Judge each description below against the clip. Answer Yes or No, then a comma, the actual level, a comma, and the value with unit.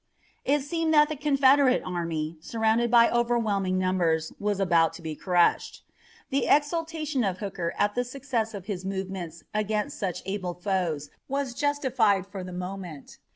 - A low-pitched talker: No, high, 205 Hz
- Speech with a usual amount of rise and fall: No, wide, 6.3 semitones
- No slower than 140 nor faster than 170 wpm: Yes, average, 155 wpm